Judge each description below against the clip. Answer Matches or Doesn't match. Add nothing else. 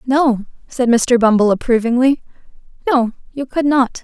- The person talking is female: Matches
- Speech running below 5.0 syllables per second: Matches